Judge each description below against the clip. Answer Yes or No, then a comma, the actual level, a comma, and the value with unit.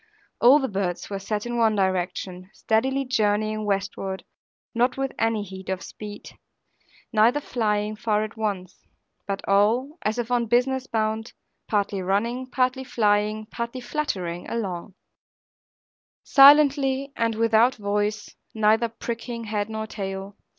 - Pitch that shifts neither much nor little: Yes, average, 3.0 semitones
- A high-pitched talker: Yes, high, 220 Hz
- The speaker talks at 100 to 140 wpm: Yes, slow, 135 wpm